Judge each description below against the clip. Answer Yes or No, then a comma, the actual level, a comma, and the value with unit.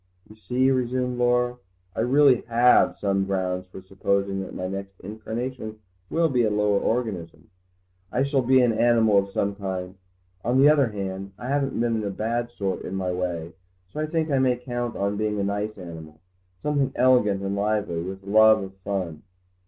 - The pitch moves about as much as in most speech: Yes, average, 4.2 semitones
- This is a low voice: Yes, low, 105 Hz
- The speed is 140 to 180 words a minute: No, average, 190 wpm